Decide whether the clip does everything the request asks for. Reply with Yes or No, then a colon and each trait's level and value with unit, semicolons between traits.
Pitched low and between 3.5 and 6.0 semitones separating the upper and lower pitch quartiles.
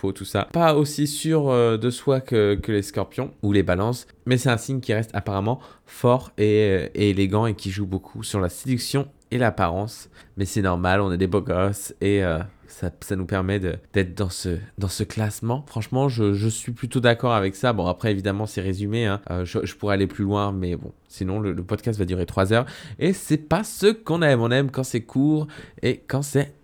Yes: low, 105 Hz; average, 4.5 semitones